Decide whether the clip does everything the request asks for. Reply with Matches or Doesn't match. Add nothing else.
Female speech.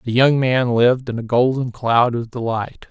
Doesn't match